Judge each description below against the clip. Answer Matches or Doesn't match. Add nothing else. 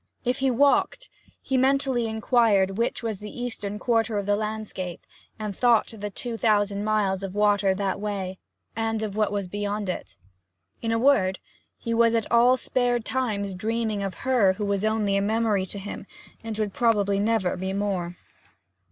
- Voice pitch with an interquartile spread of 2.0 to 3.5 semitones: Matches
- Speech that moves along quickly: Doesn't match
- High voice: Matches